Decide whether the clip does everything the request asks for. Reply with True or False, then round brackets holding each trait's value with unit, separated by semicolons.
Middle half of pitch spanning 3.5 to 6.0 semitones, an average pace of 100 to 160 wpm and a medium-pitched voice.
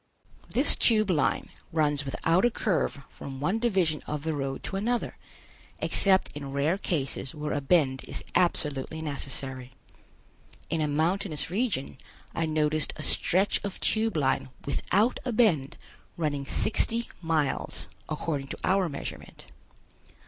True (5.2 semitones; 135 wpm; 155 Hz)